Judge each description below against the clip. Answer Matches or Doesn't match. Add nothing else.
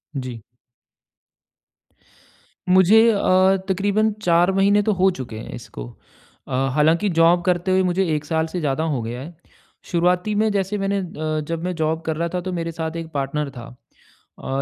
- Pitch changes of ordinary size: Matches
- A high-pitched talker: Doesn't match